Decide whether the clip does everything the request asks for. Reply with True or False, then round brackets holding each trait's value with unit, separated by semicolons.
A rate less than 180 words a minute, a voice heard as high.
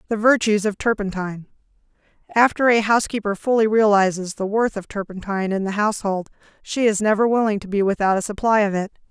True (170 wpm; 210 Hz)